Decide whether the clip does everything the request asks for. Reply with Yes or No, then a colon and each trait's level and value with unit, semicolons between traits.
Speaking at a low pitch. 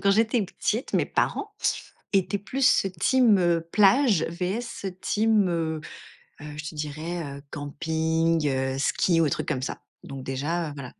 No: medium, 170 Hz